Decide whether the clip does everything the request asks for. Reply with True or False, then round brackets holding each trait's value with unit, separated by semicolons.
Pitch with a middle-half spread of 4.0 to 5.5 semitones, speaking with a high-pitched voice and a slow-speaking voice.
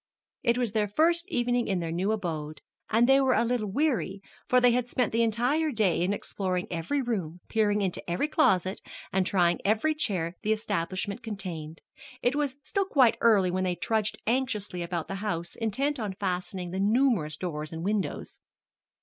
False (5.2 semitones; 210 Hz; 185 wpm)